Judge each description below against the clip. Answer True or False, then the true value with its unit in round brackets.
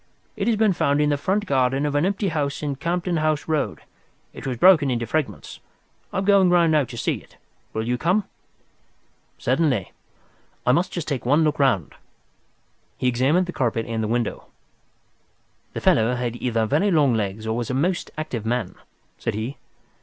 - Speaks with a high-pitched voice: False (140 Hz)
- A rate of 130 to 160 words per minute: False (185 wpm)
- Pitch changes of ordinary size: False (5.8 semitones)